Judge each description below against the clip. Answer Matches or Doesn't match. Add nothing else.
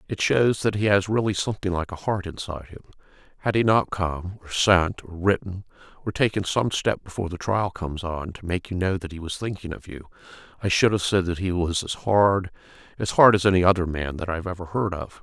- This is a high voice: Doesn't match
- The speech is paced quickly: Matches